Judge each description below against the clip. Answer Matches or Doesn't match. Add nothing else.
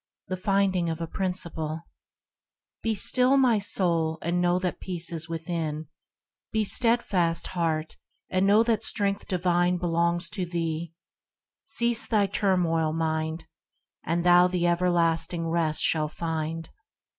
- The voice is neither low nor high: Matches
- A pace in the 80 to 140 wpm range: Matches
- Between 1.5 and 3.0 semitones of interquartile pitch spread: Matches